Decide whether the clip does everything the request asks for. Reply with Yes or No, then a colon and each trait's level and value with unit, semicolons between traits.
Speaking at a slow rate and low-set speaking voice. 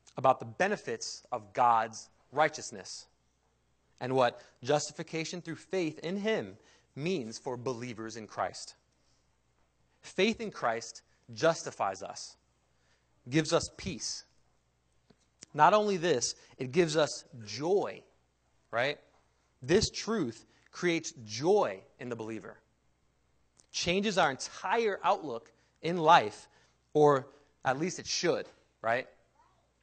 Yes: slow, 105 wpm; low, 125 Hz